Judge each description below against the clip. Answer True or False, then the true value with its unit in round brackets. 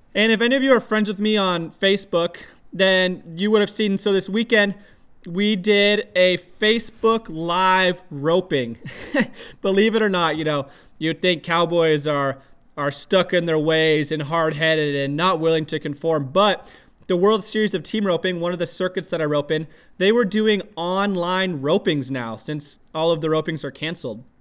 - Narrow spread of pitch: False (4.4 semitones)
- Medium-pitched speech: True (180 Hz)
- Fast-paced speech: False (185 wpm)